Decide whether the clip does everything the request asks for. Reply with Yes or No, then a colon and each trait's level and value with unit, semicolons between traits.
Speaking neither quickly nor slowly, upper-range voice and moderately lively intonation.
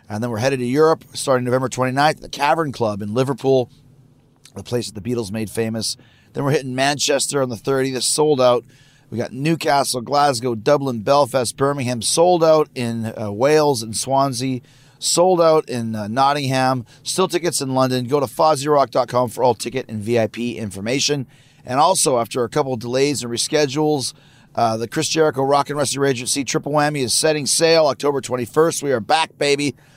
No: average, 180 wpm; low, 135 Hz; average, 3.1 semitones